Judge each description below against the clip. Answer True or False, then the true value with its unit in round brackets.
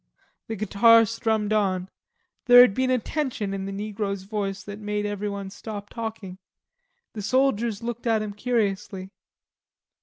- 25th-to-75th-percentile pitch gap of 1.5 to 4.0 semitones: True (2.4 semitones)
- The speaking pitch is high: True (210 Hz)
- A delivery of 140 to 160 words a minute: True (150 wpm)